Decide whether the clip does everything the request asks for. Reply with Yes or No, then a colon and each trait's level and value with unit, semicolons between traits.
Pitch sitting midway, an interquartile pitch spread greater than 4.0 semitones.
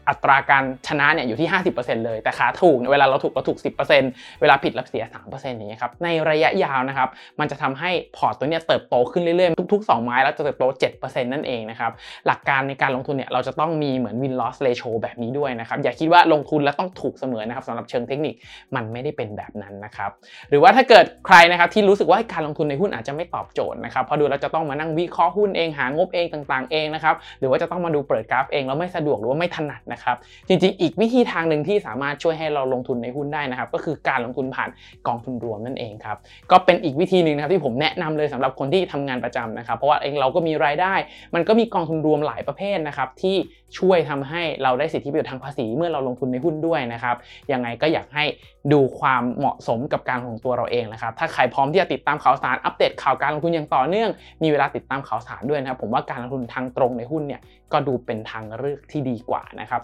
Yes: medium, 145 Hz; average, 4.7 semitones